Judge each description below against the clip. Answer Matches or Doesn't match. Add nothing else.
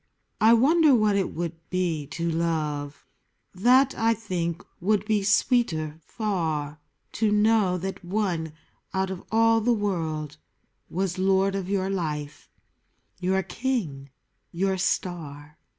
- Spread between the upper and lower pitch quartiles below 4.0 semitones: Doesn't match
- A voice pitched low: Doesn't match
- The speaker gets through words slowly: Matches